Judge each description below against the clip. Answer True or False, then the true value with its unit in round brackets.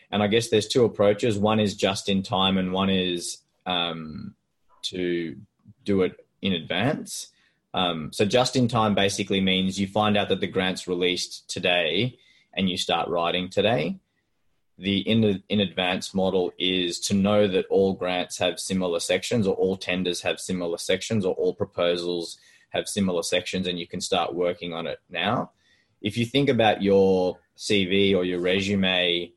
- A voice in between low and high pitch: False (95 Hz)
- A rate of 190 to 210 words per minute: False (170 wpm)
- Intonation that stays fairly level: True (2.3 semitones)